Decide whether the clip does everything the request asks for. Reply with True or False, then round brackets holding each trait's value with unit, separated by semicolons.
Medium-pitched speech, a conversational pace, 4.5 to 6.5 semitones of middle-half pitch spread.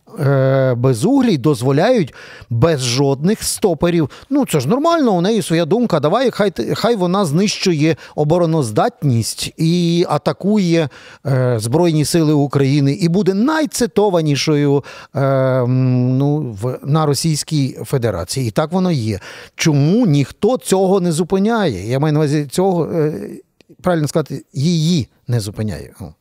True (155 Hz; 125 wpm; 4.8 semitones)